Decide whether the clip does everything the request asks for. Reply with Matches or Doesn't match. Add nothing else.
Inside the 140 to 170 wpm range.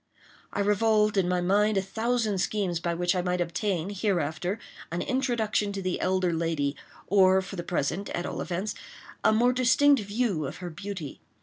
Doesn't match